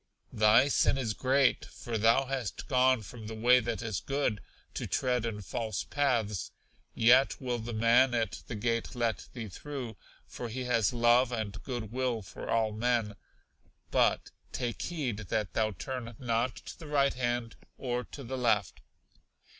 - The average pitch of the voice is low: Yes, low, 120 Hz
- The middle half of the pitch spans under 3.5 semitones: Yes, narrow, 2.5 semitones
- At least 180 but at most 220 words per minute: No, average, 165 wpm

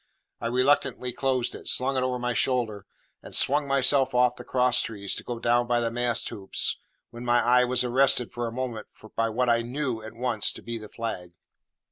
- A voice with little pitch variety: Yes, narrow, 1.5 semitones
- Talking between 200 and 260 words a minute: Yes, fast, 205 wpm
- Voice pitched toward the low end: Yes, low, 120 Hz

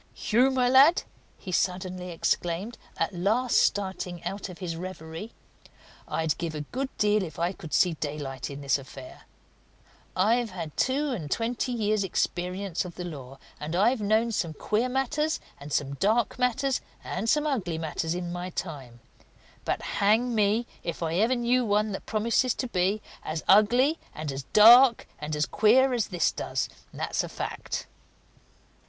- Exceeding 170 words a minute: No, average, 165 wpm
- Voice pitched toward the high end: Yes, high, 195 Hz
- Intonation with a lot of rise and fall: Yes, wide, 6.2 semitones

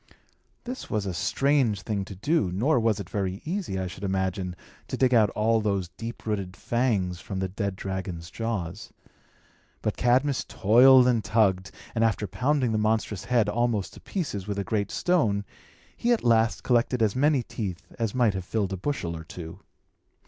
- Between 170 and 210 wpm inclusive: Yes, average, 180 wpm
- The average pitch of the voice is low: Yes, low, 105 Hz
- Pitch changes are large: No, average, 4.2 semitones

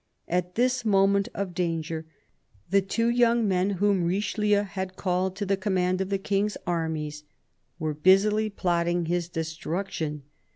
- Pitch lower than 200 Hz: Yes, high, 190 Hz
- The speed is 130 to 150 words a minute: Yes, average, 140 wpm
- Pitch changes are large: No, average, 3.0 semitones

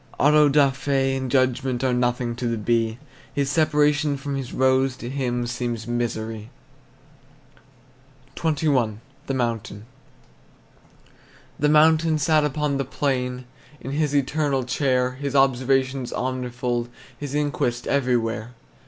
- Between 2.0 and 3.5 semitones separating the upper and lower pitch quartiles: Yes, average, 2.8 semitones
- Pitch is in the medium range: No, low, 130 Hz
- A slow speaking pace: Yes, slow, 120 wpm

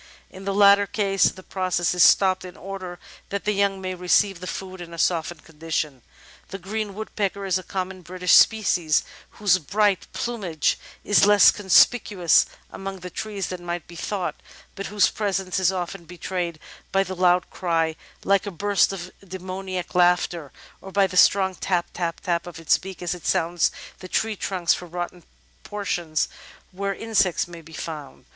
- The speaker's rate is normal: Yes, average, 180 wpm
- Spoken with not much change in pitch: Yes, narrow, 2.1 semitones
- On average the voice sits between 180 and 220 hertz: Yes, medium, 185 Hz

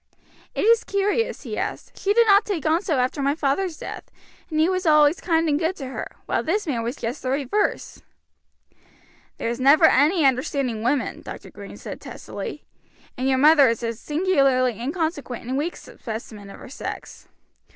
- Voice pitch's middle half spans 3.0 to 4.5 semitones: No, average, 5.0 semitones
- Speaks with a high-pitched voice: Yes, very high, 290 Hz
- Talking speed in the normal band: Yes, average, 180 wpm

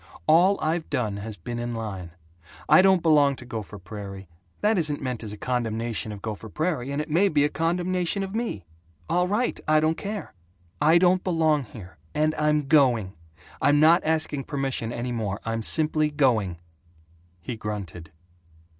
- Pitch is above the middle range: No, medium, 140 Hz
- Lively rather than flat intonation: Yes, wide, 6.5 semitones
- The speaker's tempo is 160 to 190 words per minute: Yes, average, 170 wpm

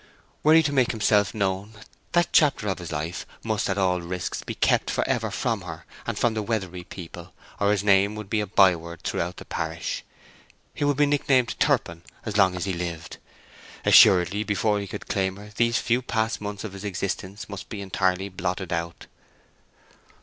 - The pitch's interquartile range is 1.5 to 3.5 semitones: Yes, average, 3.1 semitones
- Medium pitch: No, low, 100 Hz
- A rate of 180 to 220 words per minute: Yes, average, 190 wpm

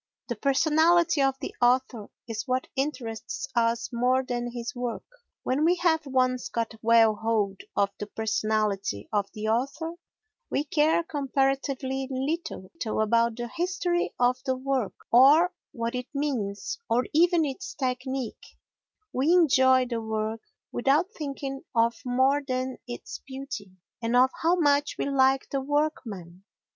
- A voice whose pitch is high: Yes, very high, 260 Hz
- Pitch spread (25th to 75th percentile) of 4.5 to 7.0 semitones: No, average, 3.5 semitones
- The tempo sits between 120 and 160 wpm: Yes, average, 140 wpm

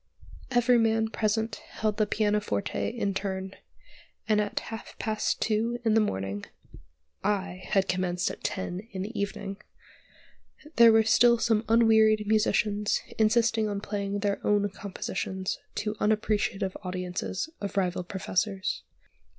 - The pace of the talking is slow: Yes, slow, 130 wpm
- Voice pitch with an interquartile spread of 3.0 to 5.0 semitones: No, narrow, 2.4 semitones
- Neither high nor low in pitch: No, high, 210 Hz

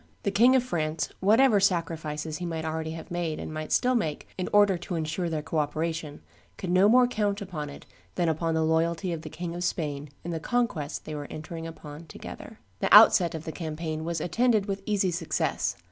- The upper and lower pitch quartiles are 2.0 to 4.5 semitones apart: Yes, average, 3.6 semitones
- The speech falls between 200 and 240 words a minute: Yes, fast, 205 wpm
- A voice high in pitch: No, medium, 165 Hz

